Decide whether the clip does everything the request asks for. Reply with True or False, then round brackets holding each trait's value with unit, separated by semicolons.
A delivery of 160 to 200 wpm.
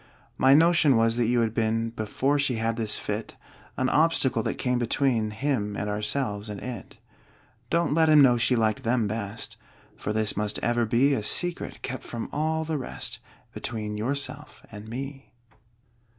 True (170 wpm)